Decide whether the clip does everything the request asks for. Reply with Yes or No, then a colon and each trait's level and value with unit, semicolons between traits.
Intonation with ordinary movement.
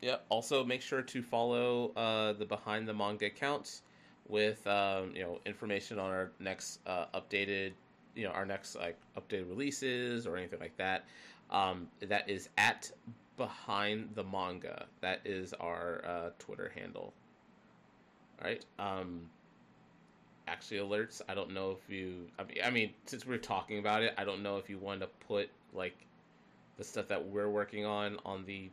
No: narrow, 2.1 semitones